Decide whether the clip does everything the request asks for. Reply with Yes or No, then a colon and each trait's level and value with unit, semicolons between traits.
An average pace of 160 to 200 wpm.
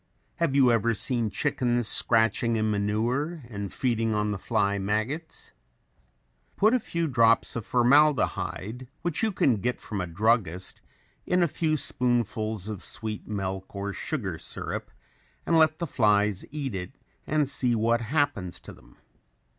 No: average, 150 wpm